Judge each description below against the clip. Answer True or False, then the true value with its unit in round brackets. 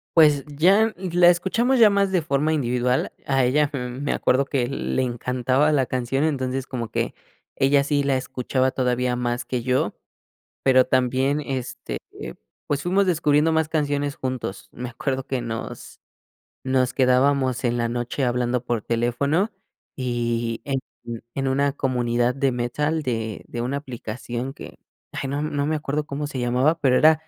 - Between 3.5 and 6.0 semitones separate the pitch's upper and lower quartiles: False (3.0 semitones)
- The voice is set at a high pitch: False (130 Hz)